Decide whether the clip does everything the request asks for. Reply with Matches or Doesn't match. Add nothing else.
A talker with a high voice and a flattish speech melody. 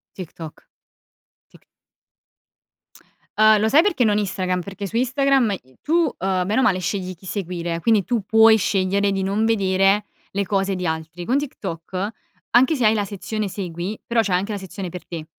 Doesn't match